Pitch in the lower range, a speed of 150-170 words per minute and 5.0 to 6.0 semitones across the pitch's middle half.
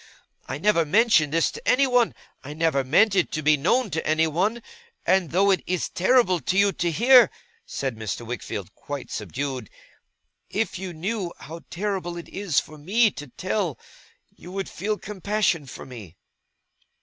No: medium, 175 Hz; average, 160 wpm; wide, 5.6 semitones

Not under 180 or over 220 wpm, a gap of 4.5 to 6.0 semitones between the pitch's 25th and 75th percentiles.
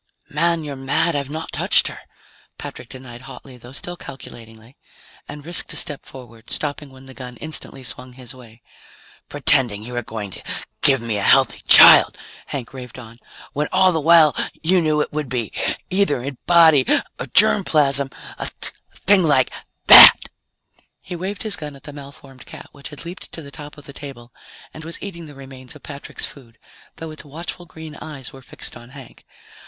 No: average, 185 wpm; average, 3.6 semitones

